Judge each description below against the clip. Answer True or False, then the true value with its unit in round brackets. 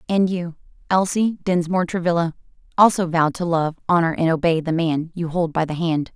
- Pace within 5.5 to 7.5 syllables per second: True (5.6 syllables/s)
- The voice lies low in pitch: False (170 Hz)